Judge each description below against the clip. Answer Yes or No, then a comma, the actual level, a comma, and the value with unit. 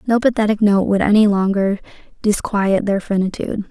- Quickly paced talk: No, average, 145 wpm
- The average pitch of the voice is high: Yes, high, 205 Hz